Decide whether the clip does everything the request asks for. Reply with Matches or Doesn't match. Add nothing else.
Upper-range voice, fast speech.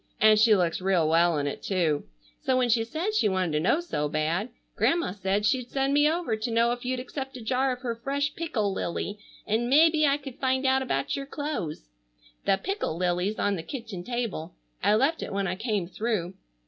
Matches